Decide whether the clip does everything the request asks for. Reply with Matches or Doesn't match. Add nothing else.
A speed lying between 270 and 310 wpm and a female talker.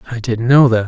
Doesn't match